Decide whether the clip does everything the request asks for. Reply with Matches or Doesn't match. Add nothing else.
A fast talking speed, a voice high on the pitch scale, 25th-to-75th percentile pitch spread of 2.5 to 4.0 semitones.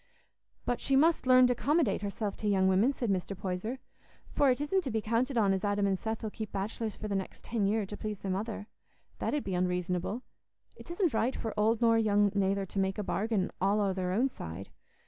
Matches